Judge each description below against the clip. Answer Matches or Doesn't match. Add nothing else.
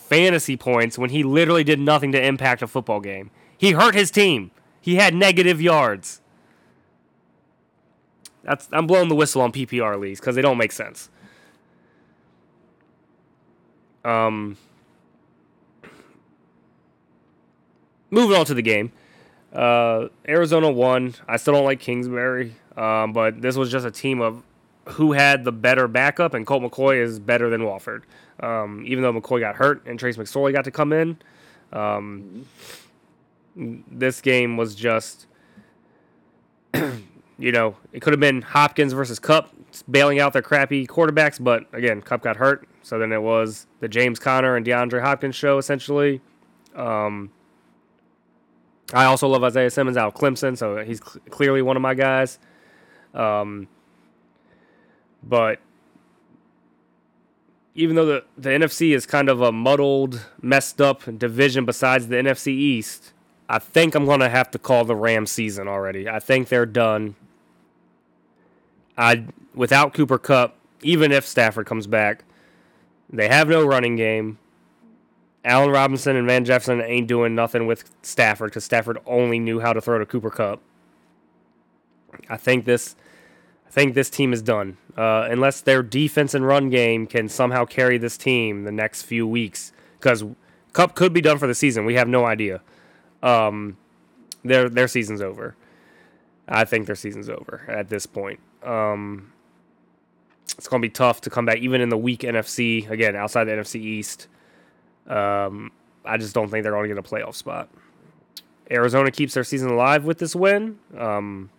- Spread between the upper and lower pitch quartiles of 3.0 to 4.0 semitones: Doesn't match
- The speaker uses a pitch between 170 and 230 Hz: Doesn't match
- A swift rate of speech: Doesn't match